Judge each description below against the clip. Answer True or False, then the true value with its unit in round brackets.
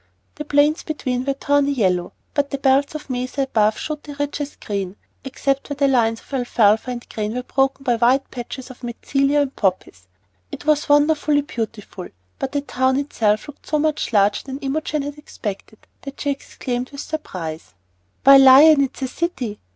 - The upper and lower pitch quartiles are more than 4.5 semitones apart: False (3.7 semitones)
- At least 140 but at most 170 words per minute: False (180 wpm)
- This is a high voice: True (270 Hz)